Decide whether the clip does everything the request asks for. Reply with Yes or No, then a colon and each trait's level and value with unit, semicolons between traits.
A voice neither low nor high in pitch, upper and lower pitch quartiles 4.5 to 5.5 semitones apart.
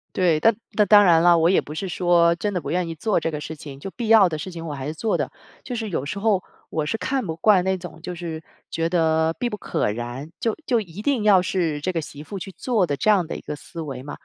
No: medium, 175 Hz; average, 4.1 semitones